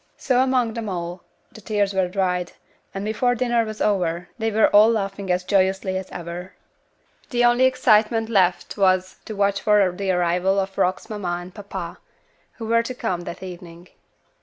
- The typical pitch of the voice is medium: No, high, 195 Hz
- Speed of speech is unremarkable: Yes, average, 175 wpm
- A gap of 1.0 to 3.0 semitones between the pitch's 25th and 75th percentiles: No, average, 3.4 semitones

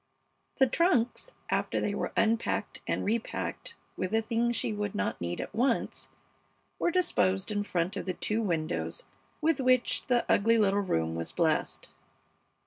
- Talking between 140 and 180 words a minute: Yes, average, 155 wpm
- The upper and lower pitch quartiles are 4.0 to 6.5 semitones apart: Yes, average, 4.4 semitones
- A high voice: Yes, high, 220 Hz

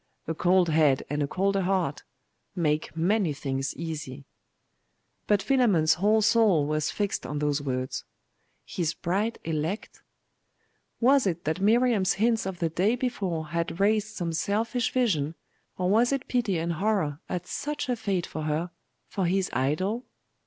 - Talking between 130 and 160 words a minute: Yes, average, 150 wpm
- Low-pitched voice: No, medium, 180 Hz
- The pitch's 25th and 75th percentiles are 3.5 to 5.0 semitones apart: No, wide, 5.5 semitones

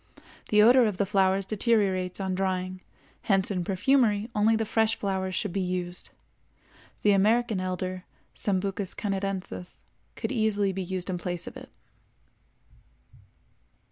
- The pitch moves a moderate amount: No, narrow, 2.3 semitones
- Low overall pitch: No, high, 195 Hz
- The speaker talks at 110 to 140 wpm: Yes, slow, 135 wpm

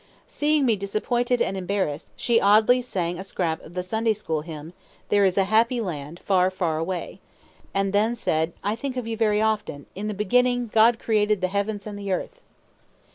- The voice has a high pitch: Yes, high, 205 Hz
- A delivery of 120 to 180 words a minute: No, average, 190 wpm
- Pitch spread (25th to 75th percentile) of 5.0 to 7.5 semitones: No, average, 3.7 semitones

